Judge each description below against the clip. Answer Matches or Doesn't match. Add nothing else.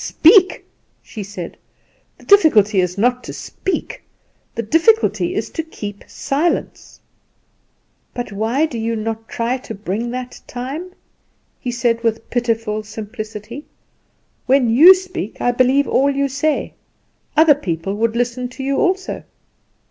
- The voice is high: Matches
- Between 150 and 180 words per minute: Doesn't match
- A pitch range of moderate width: Matches